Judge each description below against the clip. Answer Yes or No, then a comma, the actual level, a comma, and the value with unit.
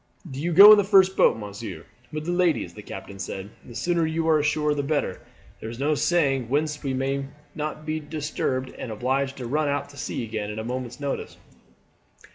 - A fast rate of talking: Yes, fast, 210 wpm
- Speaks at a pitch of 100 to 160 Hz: Yes, medium, 140 Hz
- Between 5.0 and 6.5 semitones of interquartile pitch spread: No, average, 4.3 semitones